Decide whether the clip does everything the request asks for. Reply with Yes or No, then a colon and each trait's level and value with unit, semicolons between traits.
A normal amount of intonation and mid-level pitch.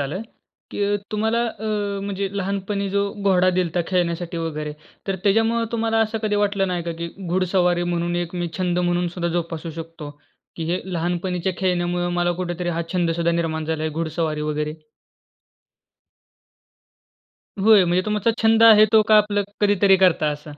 Yes: average, 3.0 semitones; medium, 180 Hz